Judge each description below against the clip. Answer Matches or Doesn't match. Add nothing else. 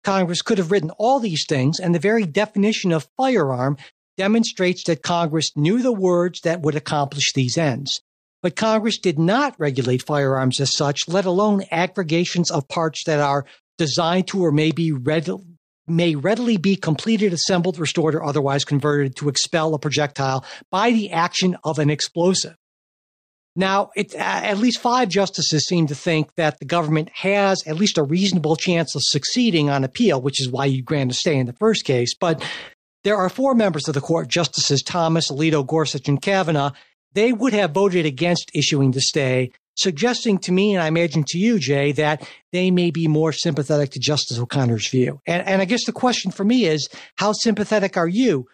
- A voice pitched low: Doesn't match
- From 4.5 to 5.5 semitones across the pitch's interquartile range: Matches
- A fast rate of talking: Doesn't match